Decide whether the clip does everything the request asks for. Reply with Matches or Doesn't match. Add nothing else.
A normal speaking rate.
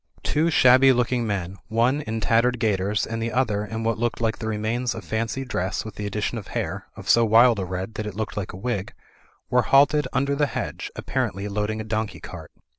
Doesn't match